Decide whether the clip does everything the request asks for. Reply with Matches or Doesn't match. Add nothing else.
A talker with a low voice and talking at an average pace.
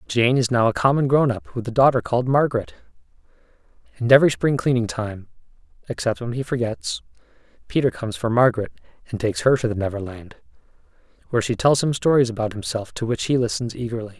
Matches